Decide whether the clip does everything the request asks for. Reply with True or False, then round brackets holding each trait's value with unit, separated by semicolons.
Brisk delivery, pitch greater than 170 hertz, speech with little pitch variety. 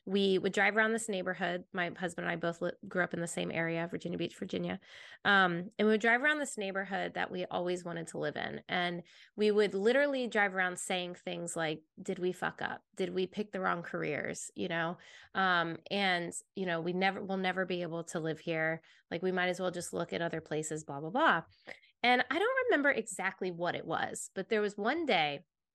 False (225 wpm; 185 Hz; 3.0 semitones)